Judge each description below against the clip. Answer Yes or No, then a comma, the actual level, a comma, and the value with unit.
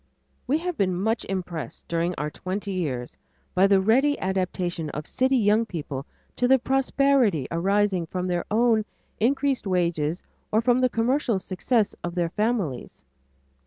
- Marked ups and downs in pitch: Yes, wide, 5.8 semitones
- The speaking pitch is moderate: No, high, 195 Hz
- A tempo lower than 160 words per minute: Yes, average, 150 wpm